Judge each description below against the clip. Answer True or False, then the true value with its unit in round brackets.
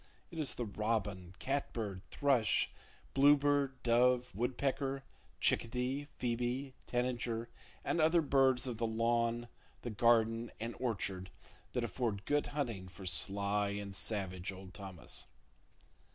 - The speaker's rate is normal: False (120 wpm)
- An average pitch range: True (4.4 semitones)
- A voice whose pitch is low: True (120 Hz)